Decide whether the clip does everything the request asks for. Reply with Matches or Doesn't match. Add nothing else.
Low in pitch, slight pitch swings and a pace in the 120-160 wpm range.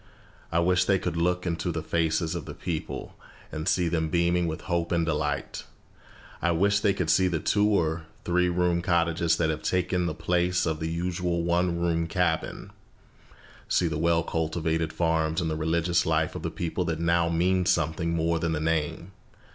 Doesn't match